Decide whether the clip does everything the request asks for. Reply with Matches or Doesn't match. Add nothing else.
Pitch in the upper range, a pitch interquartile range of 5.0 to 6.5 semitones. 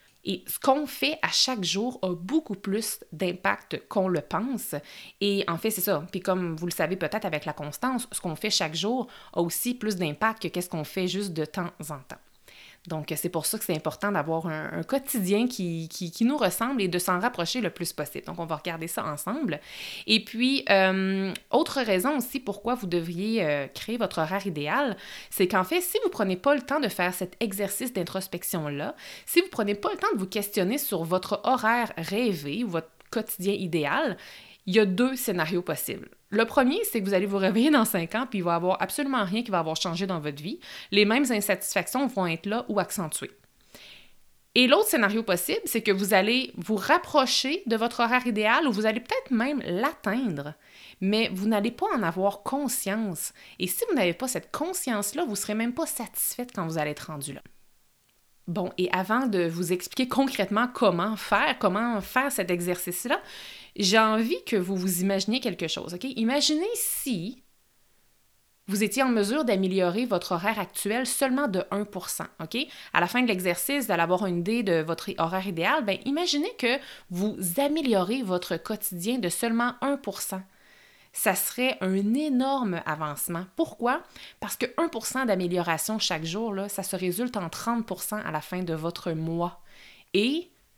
Matches